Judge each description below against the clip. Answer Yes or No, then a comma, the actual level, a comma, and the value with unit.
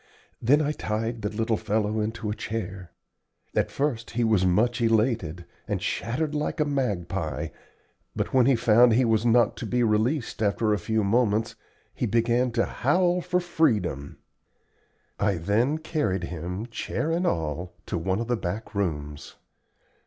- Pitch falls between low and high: No, low, 110 Hz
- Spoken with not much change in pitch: No, average, 3.7 semitones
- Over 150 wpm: Yes, average, 160 wpm